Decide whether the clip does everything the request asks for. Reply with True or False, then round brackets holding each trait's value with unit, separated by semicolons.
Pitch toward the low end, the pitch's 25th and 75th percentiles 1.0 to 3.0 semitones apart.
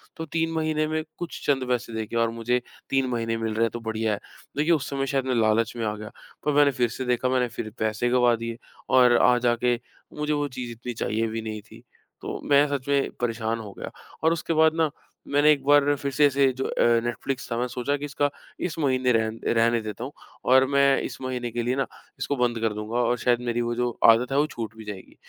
False (125 Hz; 3.5 semitones)